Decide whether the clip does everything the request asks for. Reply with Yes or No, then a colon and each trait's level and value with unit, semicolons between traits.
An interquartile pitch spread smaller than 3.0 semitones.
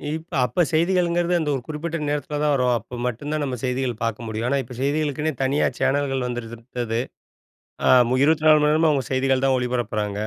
No: average, 3.7 semitones